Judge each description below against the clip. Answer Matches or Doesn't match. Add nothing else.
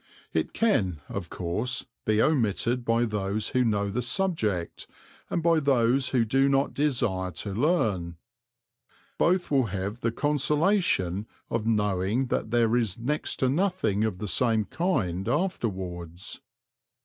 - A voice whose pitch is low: Matches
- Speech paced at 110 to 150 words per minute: Matches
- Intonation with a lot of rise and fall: Matches